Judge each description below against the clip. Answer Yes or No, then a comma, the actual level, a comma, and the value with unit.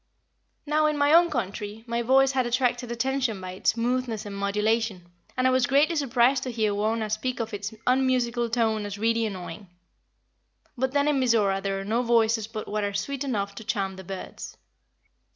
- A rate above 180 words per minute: Yes, average, 190 wpm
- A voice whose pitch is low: No, high, 230 Hz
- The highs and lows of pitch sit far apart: No, average, 3.8 semitones